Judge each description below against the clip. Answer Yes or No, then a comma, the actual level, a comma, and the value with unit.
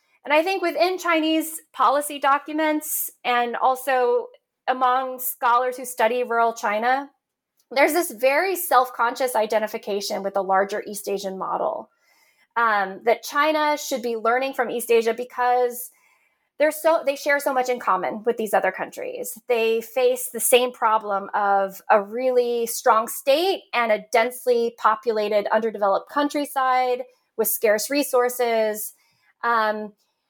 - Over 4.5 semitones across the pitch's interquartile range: No, average, 4.0 semitones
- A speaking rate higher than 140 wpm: No, slow, 135 wpm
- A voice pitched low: No, high, 245 Hz